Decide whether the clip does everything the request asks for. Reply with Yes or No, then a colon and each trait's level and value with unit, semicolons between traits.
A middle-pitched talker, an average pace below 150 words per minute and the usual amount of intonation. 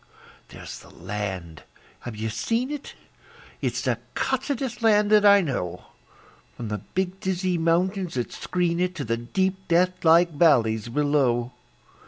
No: medium, 170 Hz; average, 140 wpm; wide, 8.3 semitones